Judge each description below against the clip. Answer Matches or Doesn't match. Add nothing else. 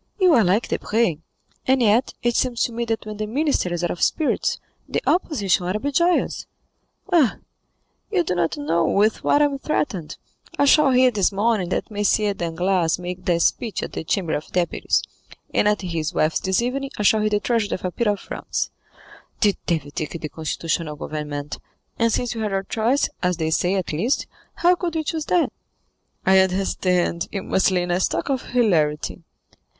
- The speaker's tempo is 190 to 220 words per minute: Matches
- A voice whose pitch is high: Matches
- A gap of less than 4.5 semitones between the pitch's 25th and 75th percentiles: Doesn't match